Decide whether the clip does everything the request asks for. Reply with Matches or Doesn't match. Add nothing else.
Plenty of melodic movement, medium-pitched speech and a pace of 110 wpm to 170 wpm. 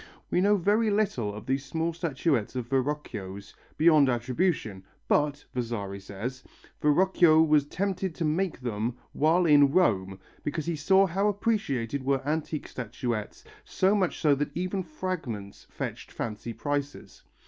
Matches